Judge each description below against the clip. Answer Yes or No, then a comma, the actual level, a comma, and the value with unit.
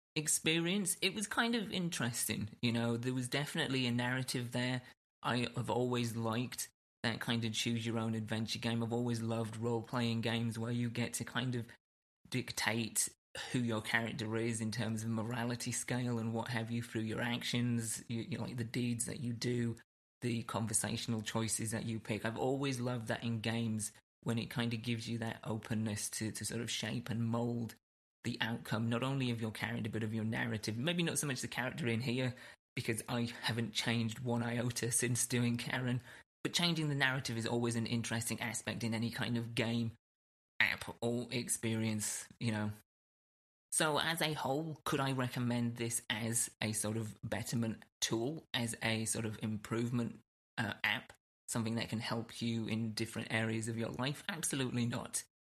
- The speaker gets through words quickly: No, average, 185 wpm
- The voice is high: No, low, 115 Hz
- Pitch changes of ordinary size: No, narrow, 1.5 semitones